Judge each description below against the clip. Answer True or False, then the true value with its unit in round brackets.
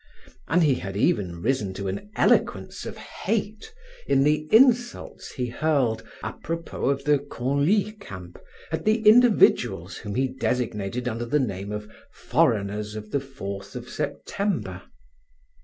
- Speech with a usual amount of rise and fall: False (7.7 semitones)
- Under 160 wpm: True (140 wpm)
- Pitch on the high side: False (130 Hz)